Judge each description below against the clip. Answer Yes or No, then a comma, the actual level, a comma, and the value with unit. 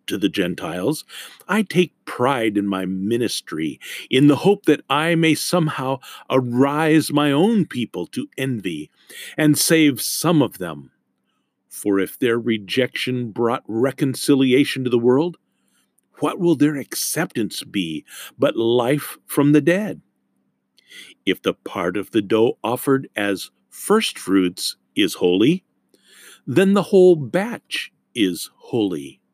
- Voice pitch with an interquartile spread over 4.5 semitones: Yes, wide, 5.5 semitones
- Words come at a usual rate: No, slow, 130 wpm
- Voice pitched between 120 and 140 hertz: Yes, low, 135 Hz